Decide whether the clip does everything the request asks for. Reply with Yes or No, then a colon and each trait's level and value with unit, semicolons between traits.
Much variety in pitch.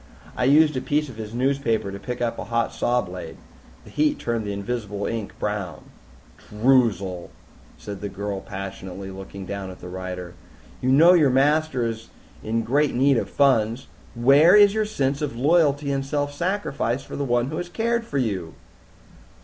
Yes: wide, 6.0 semitones